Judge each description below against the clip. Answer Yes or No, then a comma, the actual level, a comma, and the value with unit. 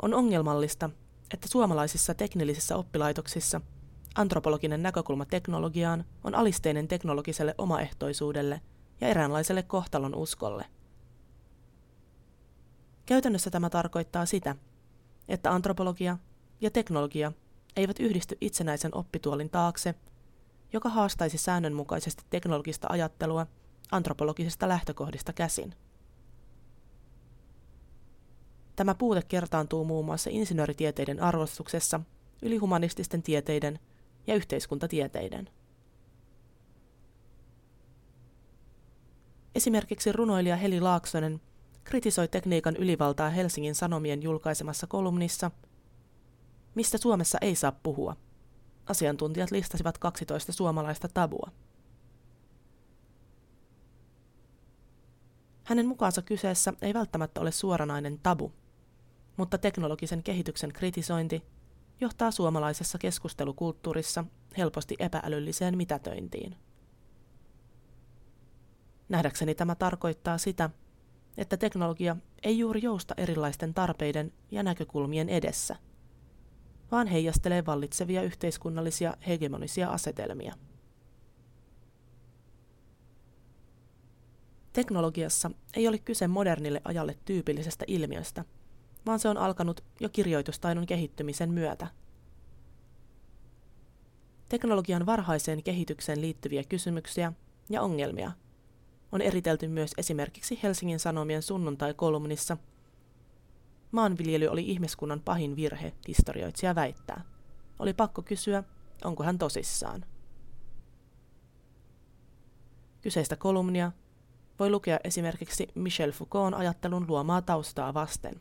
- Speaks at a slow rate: Yes, slow, 85 wpm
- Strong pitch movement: Yes, wide, 5.7 semitones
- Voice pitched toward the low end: No, medium, 160 Hz